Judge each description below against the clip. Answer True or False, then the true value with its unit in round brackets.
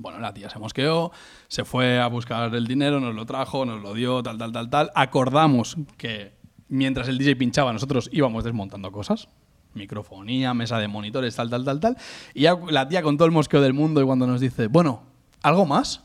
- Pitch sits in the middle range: False (130 Hz)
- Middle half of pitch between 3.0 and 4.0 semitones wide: True (3.6 semitones)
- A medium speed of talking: False (205 wpm)